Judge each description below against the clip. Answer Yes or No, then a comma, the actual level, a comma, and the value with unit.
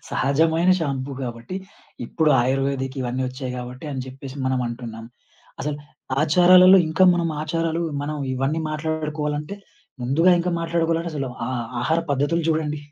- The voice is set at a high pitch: No, medium, 150 Hz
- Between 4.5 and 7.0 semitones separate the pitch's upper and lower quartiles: No, average, 3.9 semitones